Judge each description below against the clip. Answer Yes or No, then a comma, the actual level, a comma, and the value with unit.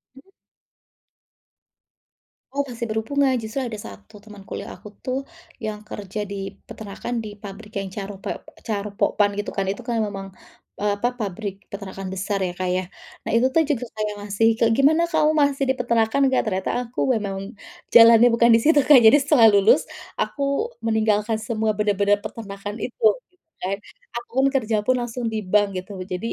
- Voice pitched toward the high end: Yes, high, 220 Hz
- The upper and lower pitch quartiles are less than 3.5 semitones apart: Yes, average, 3.1 semitones